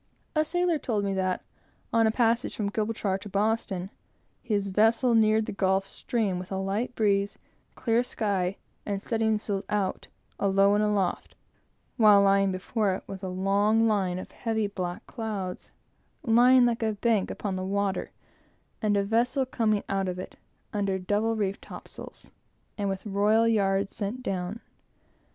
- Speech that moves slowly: No, average, 155 wpm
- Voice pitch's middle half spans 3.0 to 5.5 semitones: No, narrow, 2.5 semitones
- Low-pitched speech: No, high, 205 Hz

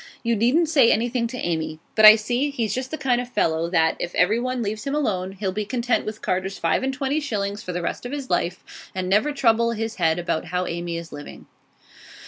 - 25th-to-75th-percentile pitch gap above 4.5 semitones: Yes, wide, 5.6 semitones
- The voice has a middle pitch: No, high, 215 Hz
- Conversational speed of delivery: No, fast, 225 wpm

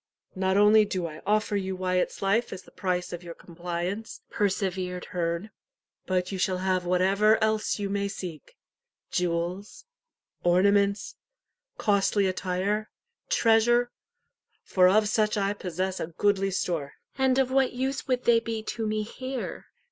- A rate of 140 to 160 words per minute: Yes, average, 150 wpm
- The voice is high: Yes, high, 195 Hz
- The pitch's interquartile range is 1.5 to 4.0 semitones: Yes, average, 2.9 semitones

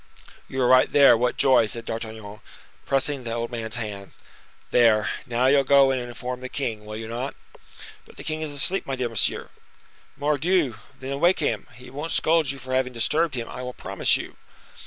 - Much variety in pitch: No, average, 3.2 semitones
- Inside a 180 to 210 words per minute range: Yes, average, 195 wpm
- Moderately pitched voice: No, low, 125 Hz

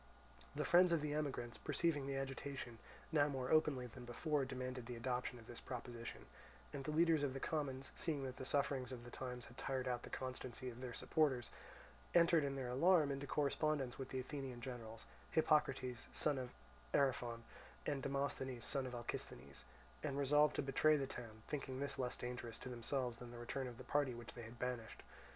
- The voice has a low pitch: Yes, low, 130 Hz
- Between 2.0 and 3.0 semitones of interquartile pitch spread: Yes, average, 2.7 semitones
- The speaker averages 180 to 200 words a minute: Yes, average, 190 wpm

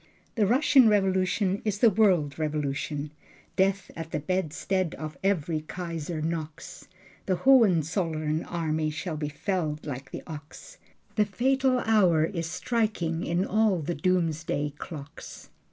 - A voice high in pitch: No, medium, 170 Hz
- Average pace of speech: No, slow, 130 wpm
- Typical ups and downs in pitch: Yes, average, 4.2 semitones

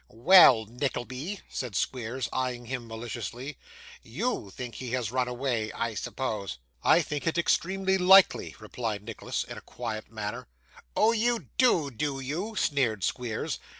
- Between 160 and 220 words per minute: No, average, 145 wpm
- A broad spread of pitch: Yes, wide, 5.9 semitones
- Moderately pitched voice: No, low, 125 Hz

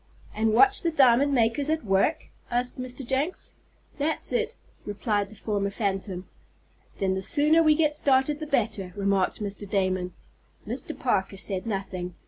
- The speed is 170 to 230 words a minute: No, average, 150 wpm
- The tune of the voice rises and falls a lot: Yes, wide, 6.7 semitones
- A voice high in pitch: Yes, high, 225 Hz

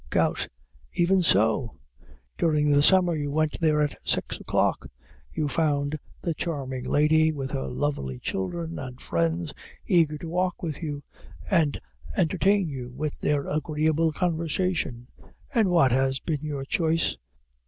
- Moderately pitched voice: Yes, medium, 150 Hz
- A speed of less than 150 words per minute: Yes, average, 140 wpm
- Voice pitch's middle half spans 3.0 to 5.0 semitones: Yes, average, 3.4 semitones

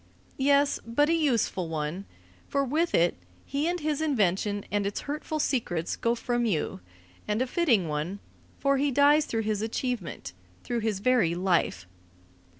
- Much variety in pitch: Yes, wide, 6.7 semitones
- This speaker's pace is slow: No, average, 155 wpm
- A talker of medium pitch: No, high, 230 Hz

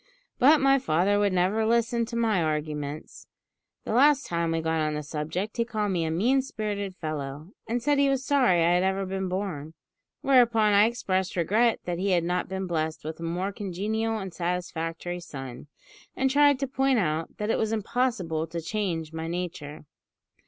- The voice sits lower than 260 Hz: Yes, high, 190 Hz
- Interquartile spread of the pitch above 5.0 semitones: Yes, wide, 5.5 semitones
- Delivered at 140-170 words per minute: No, average, 190 wpm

